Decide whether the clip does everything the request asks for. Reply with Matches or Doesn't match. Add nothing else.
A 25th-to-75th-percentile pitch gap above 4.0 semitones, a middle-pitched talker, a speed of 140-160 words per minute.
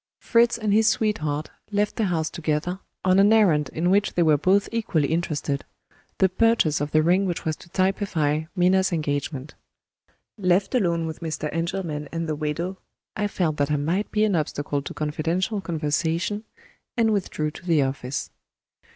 Doesn't match